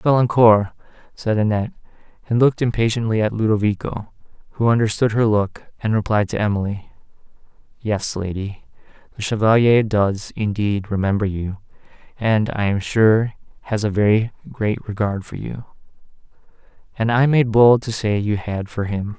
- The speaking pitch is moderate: No, low, 110 Hz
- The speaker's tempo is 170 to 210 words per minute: No, average, 140 wpm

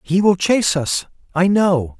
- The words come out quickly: No, average, 180 wpm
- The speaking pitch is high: No, medium, 180 Hz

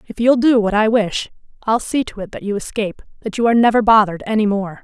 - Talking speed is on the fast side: Yes, fast, 235 wpm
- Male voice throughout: No, female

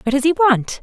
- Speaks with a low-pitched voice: No, very high, 285 Hz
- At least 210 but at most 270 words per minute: No, fast, 290 wpm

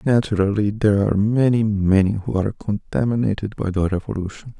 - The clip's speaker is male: Yes, male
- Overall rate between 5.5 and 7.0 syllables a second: Yes, 5.8 syllables/s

